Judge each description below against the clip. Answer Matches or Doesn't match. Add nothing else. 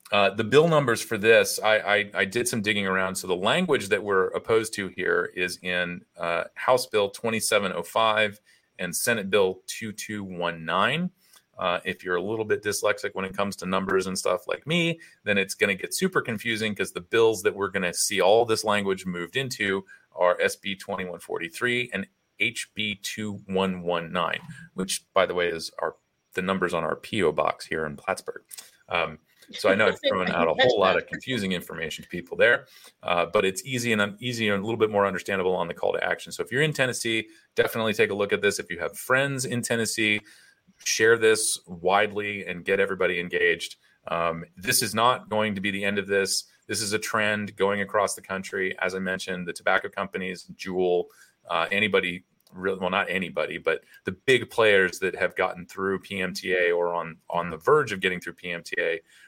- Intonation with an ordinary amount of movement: Matches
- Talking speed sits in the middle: Doesn't match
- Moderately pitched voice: Doesn't match